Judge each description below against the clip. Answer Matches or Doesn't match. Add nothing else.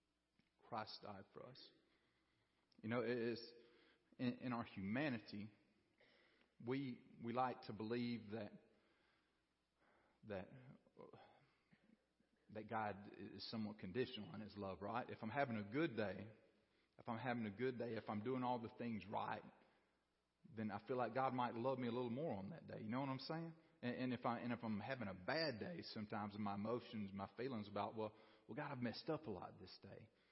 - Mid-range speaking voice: Doesn't match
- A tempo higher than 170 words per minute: Matches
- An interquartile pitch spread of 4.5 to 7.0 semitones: Doesn't match